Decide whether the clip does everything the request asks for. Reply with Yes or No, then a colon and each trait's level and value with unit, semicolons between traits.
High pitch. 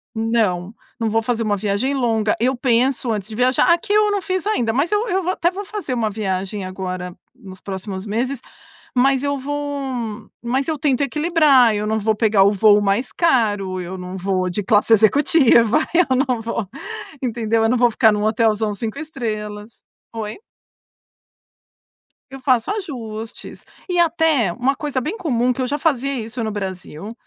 Yes: high, 230 Hz